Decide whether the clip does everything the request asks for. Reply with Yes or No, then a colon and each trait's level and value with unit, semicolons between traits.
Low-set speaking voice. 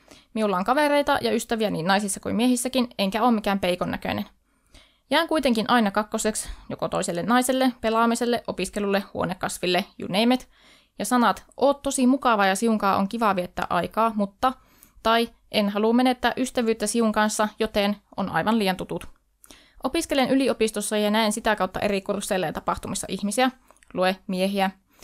No: high, 220 Hz